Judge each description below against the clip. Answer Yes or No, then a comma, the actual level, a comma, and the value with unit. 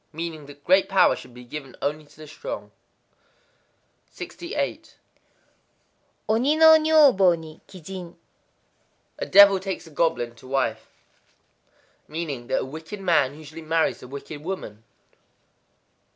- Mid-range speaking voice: Yes, medium, 160 Hz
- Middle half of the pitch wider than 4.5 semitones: Yes, average, 5.1 semitones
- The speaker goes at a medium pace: No, slow, 125 wpm